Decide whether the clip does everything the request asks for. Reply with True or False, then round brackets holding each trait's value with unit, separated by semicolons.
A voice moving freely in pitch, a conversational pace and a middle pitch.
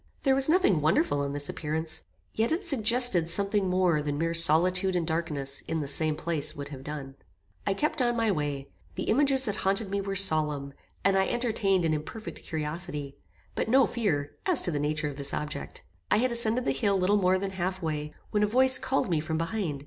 False (6.0 semitones; 210 wpm; 175 Hz)